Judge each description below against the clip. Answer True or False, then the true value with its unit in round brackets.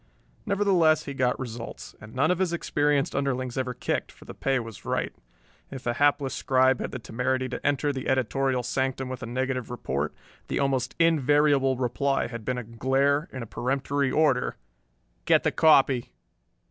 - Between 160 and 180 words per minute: True (170 wpm)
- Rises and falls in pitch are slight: True (2.2 semitones)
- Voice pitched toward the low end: True (130 Hz)